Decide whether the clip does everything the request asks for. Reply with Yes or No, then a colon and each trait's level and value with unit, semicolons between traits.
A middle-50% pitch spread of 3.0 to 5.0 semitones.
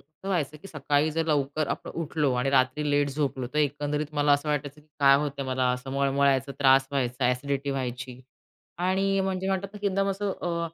No: narrow, 2.5 semitones